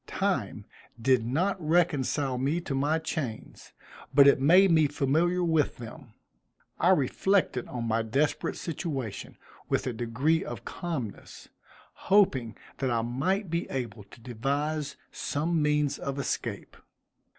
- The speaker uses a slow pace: Yes, slow, 130 wpm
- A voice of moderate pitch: Yes, medium, 145 Hz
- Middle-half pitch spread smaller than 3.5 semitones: No, average, 4.6 semitones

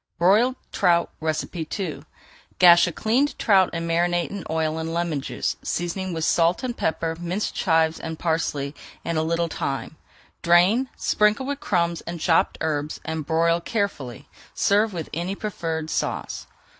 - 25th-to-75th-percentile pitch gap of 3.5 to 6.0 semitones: No, average, 2.8 semitones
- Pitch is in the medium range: Yes, medium, 170 Hz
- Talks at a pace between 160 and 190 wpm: No, average, 150 wpm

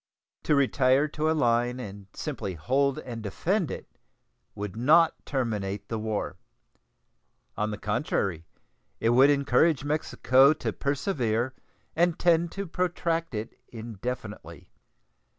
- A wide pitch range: Yes, wide, 5.8 semitones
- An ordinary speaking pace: No, slow, 120 wpm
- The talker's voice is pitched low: Yes, low, 130 Hz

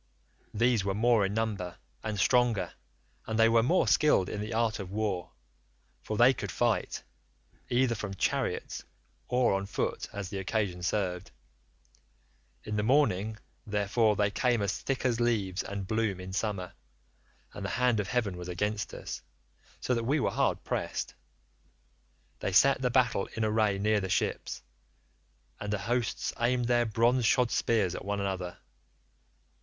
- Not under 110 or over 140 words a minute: No, average, 160 wpm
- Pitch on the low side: Yes, low, 105 Hz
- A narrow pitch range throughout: No, average, 3.4 semitones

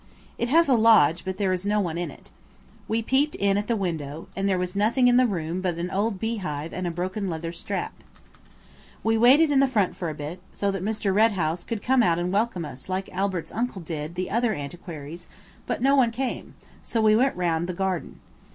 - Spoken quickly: Yes, fast, 225 wpm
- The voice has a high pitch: Yes, high, 195 Hz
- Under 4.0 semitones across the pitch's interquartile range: No, average, 4.6 semitones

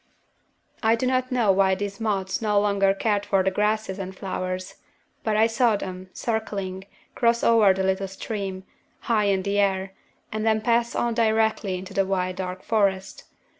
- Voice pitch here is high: Yes, high, 200 Hz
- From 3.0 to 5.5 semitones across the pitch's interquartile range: No, narrow, 2.5 semitones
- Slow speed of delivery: No, average, 170 wpm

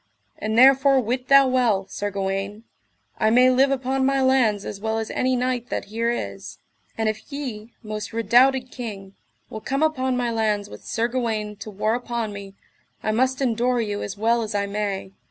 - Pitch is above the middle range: Yes, high, 230 Hz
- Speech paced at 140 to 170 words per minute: No, average, 190 wpm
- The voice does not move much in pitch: No, average, 3.4 semitones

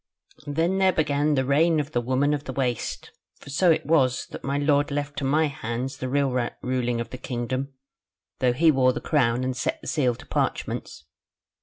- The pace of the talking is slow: No, average, 200 wpm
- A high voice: No, low, 135 Hz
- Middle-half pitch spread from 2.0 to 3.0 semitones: Yes, narrow, 2.5 semitones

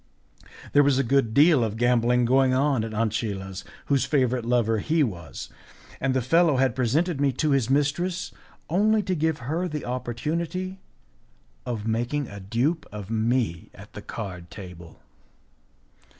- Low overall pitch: Yes, low, 130 Hz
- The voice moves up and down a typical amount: Yes, average, 4.8 semitones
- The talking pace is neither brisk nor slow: Yes, average, 150 wpm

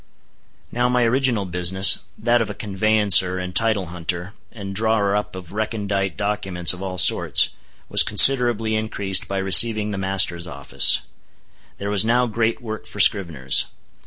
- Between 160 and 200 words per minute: No, average, 140 wpm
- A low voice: Yes, low, 100 Hz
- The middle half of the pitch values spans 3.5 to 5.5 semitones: No, average, 3.0 semitones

